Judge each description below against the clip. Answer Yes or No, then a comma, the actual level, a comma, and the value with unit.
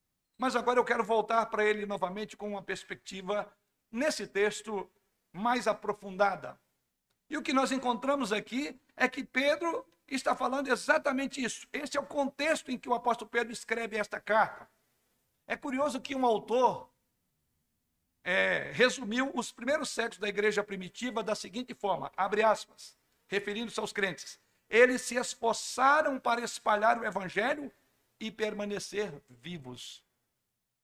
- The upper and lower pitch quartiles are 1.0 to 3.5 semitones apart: No, average, 3.9 semitones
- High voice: Yes, high, 230 Hz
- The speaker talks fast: No, average, 140 wpm